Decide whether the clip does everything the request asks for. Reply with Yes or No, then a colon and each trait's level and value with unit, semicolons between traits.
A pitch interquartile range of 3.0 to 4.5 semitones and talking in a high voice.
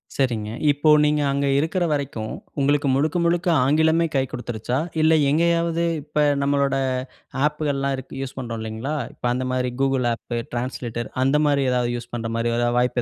No: average, 3.7 semitones; low, 135 Hz